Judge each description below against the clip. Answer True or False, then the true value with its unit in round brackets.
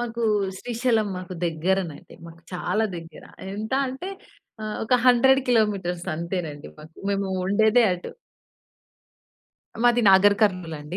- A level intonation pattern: False (4.9 semitones)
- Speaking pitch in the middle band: False (195 Hz)